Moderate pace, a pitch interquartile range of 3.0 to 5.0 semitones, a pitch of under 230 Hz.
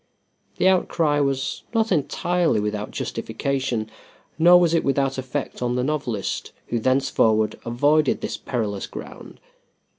No: slow, 125 wpm; average, 4.7 semitones; low, 135 Hz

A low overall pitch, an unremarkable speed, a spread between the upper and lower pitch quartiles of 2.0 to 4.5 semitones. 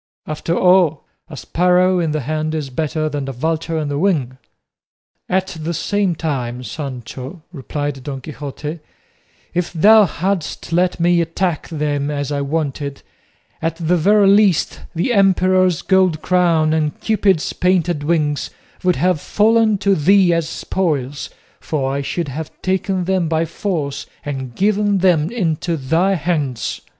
No: medium, 165 Hz; average, 145 wpm; average, 4.0 semitones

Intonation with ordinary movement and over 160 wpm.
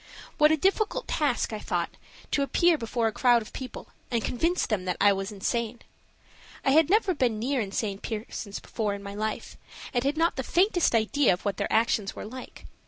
No: wide, 5.7 semitones; average, 200 wpm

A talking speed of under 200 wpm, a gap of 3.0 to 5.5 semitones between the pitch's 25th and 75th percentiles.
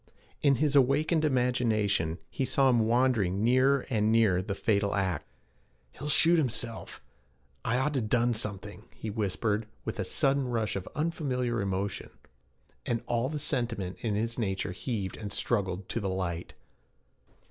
Yes: average, 150 wpm; average, 4.4 semitones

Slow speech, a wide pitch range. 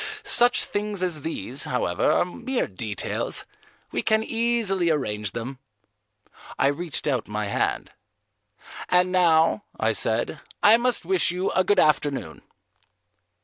Yes: slow, 130 wpm; wide, 8.0 semitones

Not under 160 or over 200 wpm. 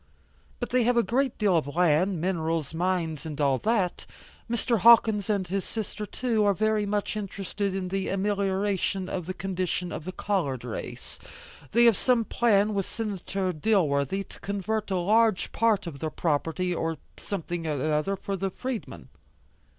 Yes: average, 165 wpm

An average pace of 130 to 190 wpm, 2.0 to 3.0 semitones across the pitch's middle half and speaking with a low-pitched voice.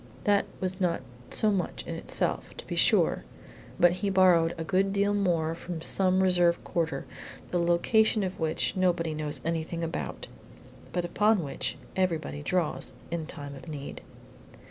No: average, 155 wpm; narrow, 2.6 semitones; medium, 175 Hz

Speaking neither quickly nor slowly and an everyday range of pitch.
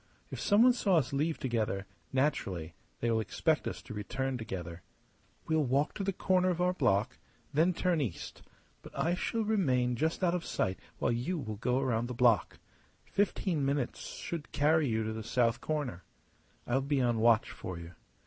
No: average, 180 wpm; wide, 6.5 semitones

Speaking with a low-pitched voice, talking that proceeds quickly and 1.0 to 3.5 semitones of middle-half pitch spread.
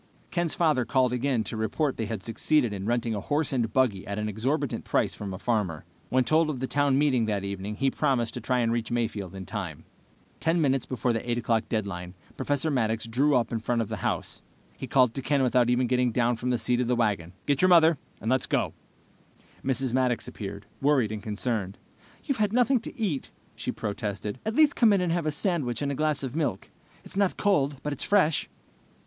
No: low, 125 Hz; fast, 220 wpm; average, 4.8 semitones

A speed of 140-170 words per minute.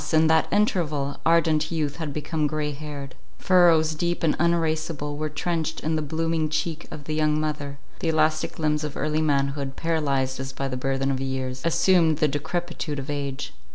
No: average, 180 wpm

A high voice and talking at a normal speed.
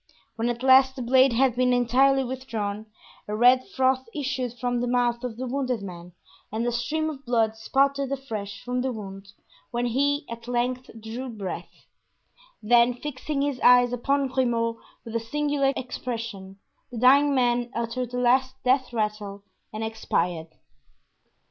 Yes: high, 245 Hz; average, 155 wpm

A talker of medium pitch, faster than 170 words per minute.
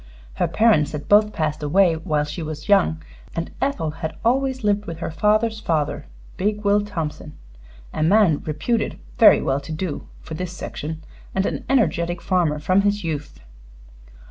No: medium, 170 Hz; average, 165 wpm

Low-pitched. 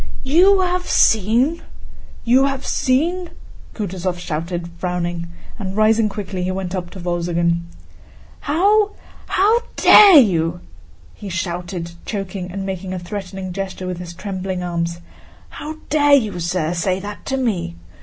No: high, 190 Hz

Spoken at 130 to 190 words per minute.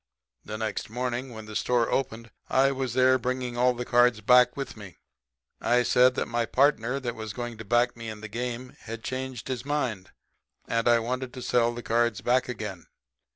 No: average, 200 wpm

